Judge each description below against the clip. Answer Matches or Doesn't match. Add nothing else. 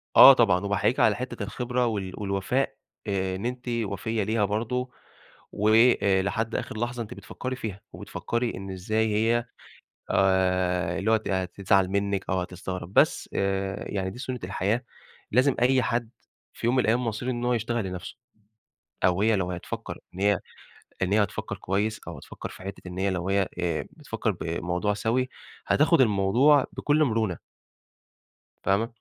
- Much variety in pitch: Doesn't match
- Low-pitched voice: Matches